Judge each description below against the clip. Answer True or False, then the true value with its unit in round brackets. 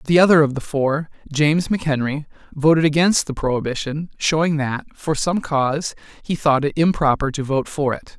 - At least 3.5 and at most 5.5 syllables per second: True (5.4 syllables/s)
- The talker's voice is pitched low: False (150 Hz)